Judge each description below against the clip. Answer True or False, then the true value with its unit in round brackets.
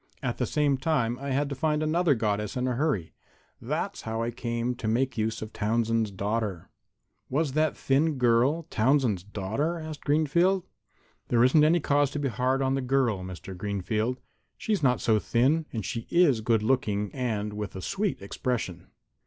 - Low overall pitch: True (125 Hz)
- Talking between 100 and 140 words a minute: False (175 wpm)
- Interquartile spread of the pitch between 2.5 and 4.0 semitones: False (5.0 semitones)